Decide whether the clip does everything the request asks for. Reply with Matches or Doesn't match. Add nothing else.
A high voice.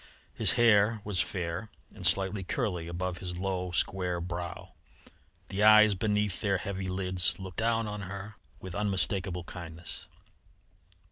Doesn't match